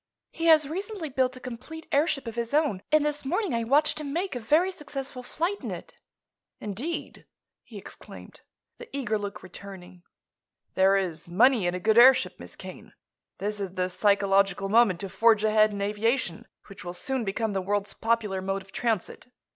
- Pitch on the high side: Yes, high, 225 Hz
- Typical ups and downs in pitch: No, wide, 6.1 semitones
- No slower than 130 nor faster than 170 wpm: No, average, 180 wpm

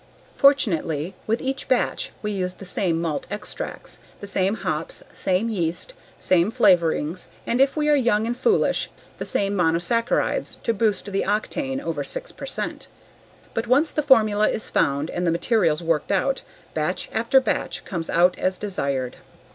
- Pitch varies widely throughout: Yes, wide, 5.8 semitones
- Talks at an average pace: Yes, average, 160 wpm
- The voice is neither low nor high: No, high, 205 Hz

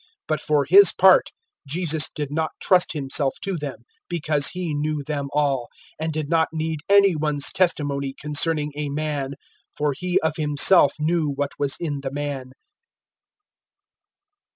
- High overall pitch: No, medium, 150 Hz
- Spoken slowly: No, average, 155 wpm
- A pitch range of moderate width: No, narrow, 2.1 semitones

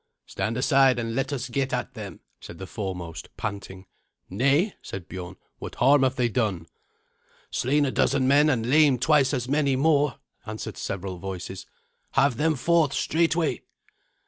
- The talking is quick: No, average, 155 wpm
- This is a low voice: Yes, low, 130 Hz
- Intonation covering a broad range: Yes, wide, 5.9 semitones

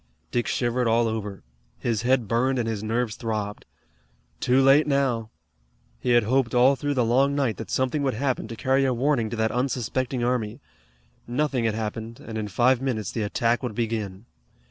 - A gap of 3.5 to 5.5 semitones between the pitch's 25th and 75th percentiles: No, average, 2.8 semitones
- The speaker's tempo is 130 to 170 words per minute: No, average, 185 wpm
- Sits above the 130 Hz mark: No, low, 120 Hz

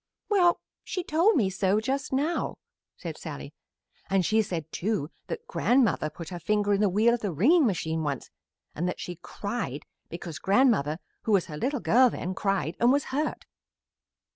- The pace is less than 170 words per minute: No, average, 175 wpm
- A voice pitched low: No, high, 205 Hz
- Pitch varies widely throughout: Yes, wide, 7.1 semitones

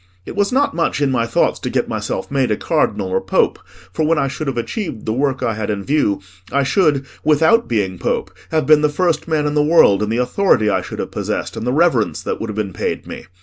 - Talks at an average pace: No, fast, 250 wpm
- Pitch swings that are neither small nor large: No, wide, 6.2 semitones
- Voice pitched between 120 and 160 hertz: Yes, low, 135 Hz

